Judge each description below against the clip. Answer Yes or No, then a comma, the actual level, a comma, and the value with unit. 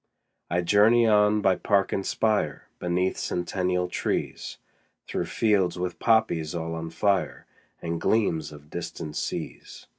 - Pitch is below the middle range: Yes, very low, 90 Hz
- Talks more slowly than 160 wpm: Yes, average, 140 wpm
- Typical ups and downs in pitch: Yes, average, 3.7 semitones